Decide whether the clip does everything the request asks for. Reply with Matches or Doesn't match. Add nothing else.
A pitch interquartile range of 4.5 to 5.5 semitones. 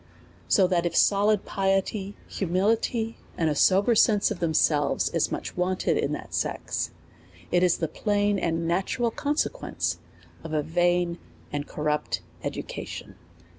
Doesn't match